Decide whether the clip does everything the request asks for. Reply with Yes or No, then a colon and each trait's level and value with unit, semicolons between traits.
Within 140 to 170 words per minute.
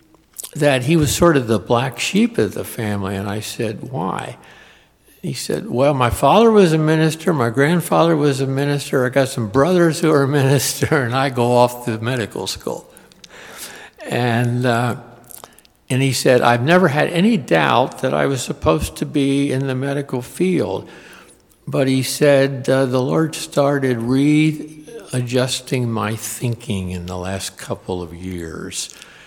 Yes: average, 160 wpm